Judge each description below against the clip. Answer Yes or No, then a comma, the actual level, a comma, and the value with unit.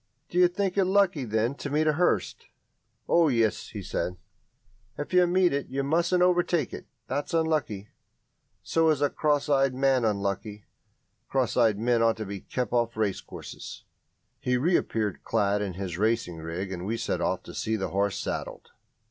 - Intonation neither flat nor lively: No, wide, 7.0 semitones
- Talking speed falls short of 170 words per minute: No, average, 175 wpm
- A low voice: Yes, low, 125 Hz